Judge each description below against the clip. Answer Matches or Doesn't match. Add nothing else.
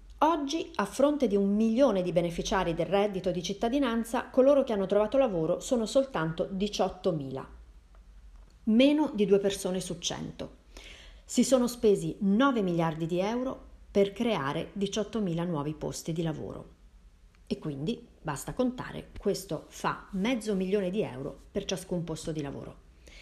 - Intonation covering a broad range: Matches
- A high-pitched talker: Matches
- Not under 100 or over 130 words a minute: Doesn't match